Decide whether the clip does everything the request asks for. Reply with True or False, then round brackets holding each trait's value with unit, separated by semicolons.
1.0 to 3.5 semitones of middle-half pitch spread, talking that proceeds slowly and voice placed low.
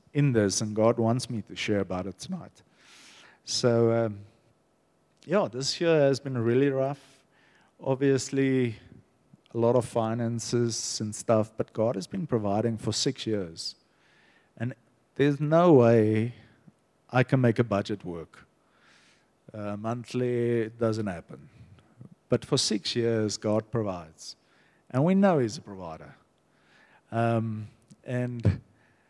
True (3.1 semitones; 130 wpm; 115 Hz)